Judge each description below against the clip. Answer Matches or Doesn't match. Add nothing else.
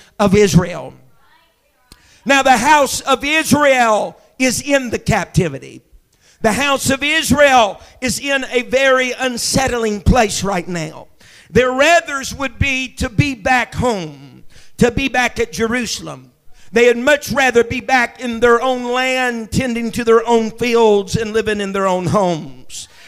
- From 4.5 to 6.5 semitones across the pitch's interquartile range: Doesn't match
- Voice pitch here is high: Matches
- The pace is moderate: Matches